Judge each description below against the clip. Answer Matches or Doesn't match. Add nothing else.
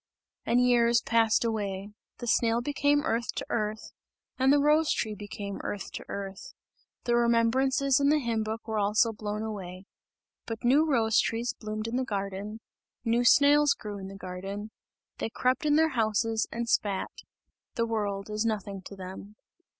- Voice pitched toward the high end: Matches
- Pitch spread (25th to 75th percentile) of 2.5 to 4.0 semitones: Matches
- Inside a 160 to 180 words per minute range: Matches